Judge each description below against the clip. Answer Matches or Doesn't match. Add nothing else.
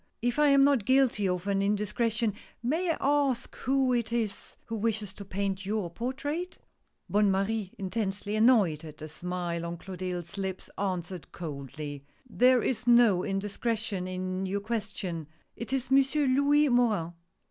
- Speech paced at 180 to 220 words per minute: Doesn't match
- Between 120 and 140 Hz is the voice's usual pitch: Doesn't match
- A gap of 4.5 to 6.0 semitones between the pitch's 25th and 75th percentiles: Matches